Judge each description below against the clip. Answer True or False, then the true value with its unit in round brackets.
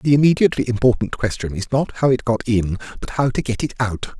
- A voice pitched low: True (120 Hz)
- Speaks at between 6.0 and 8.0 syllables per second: True (6.1 syllables/s)